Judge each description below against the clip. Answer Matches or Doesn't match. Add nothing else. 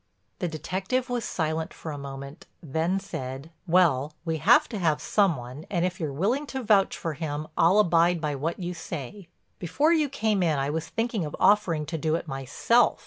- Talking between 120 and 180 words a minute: Doesn't match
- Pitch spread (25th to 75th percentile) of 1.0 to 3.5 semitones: Doesn't match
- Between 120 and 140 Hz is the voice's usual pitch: Doesn't match